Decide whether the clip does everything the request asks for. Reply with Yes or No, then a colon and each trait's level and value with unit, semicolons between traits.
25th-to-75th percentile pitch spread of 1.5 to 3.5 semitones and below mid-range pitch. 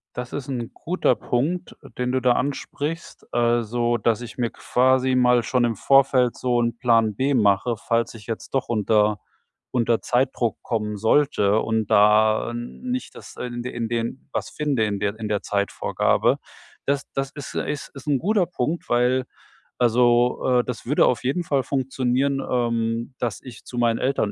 Yes: average, 2.7 semitones; low, 120 Hz